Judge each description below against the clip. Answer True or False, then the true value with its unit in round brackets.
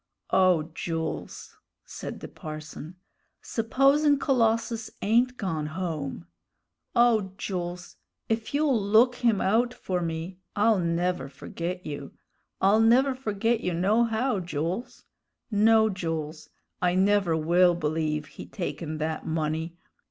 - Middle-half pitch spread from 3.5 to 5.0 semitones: False (5.6 semitones)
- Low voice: False (185 Hz)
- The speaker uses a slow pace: True (115 wpm)